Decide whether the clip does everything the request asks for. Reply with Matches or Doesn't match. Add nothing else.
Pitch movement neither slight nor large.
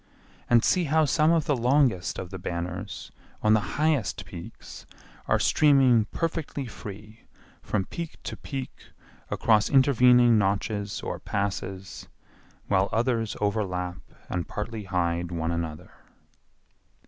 Doesn't match